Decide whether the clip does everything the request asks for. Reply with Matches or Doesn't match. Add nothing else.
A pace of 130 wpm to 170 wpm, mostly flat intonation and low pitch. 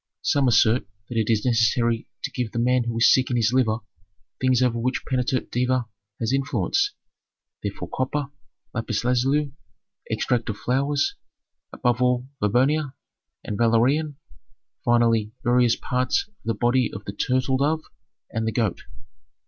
Matches